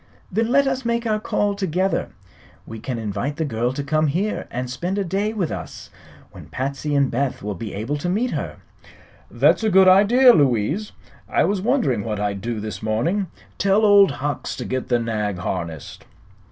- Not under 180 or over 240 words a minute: Yes, average, 190 wpm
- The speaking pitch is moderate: Yes, medium, 145 Hz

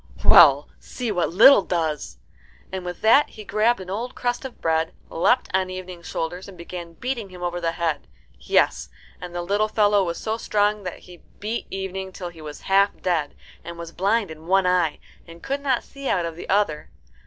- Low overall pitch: No, medium, 185 Hz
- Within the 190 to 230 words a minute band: Yes, average, 195 wpm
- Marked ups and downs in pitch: No, average, 3.8 semitones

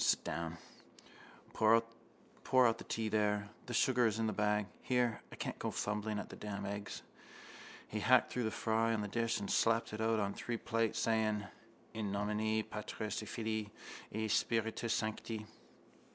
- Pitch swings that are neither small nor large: No, narrow, 1.4 semitones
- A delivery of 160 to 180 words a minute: Yes, average, 170 wpm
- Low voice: Yes, low, 110 Hz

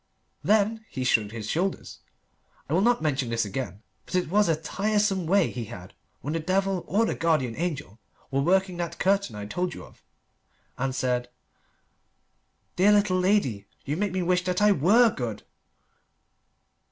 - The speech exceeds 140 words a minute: Yes, average, 165 wpm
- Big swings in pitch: Yes, wide, 7.3 semitones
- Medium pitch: Yes, medium, 175 Hz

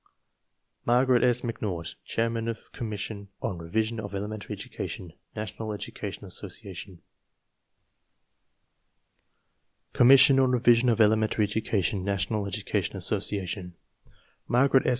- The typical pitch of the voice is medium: No, low, 110 Hz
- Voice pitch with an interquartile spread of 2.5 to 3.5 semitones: Yes, average, 2.9 semitones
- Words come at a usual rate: No, slow, 110 wpm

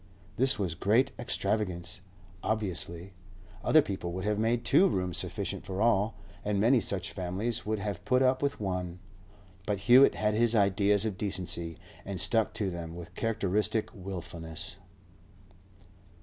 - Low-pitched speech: Yes, low, 100 Hz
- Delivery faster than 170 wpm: No, average, 145 wpm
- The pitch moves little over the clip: No, average, 3.4 semitones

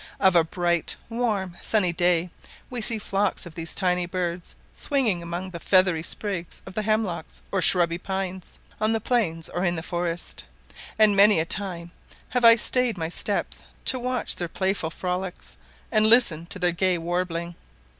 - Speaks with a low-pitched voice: No, medium, 185 Hz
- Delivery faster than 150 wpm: Yes, average, 170 wpm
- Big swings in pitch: No, average, 3.5 semitones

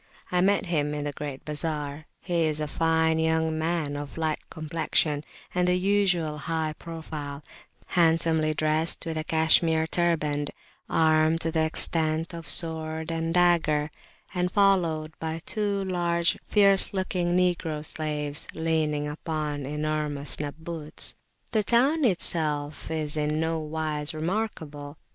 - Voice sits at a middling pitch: Yes, medium, 160 Hz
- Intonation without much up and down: Yes, narrow, 2.0 semitones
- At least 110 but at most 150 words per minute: Yes, slow, 135 wpm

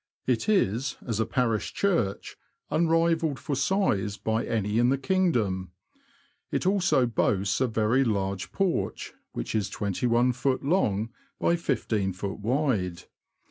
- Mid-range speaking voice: No, low, 120 Hz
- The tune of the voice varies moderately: No, wide, 6.8 semitones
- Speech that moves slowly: Yes, slow, 130 wpm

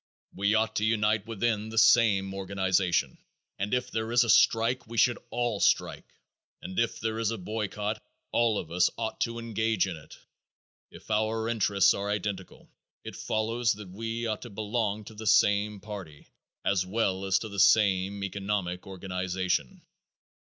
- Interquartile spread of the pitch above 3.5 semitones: No, narrow, 2.6 semitones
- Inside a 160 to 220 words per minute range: Yes, average, 165 wpm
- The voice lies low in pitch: Yes, low, 105 Hz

